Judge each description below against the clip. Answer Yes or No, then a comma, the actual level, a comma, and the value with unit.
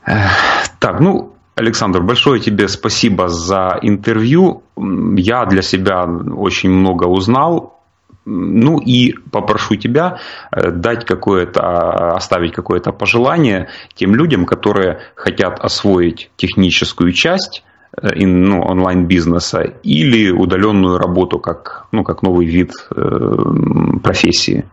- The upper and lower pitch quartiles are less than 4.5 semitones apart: Yes, average, 2.8 semitones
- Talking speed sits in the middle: No, slow, 105 wpm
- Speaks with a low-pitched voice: Yes, very low, 95 Hz